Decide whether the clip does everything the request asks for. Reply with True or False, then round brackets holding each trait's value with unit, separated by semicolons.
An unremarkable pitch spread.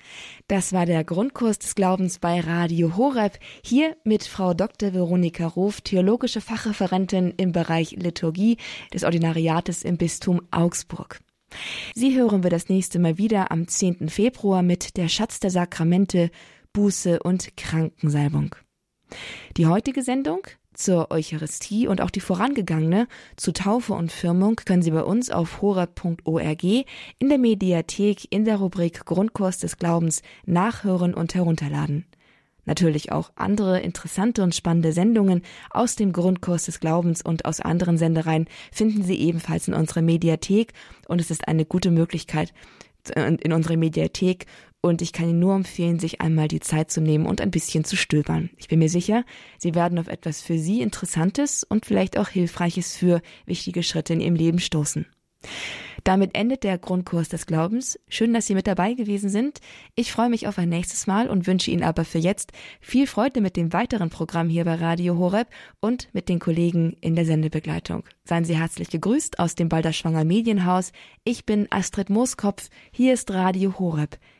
True (3.6 semitones)